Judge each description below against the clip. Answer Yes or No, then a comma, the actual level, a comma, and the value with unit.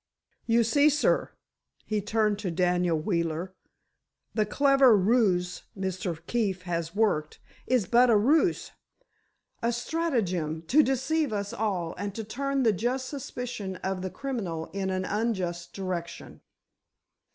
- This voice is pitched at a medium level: No, high, 205 Hz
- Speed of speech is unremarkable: No, slow, 130 wpm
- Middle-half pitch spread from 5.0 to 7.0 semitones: Yes, wide, 5.4 semitones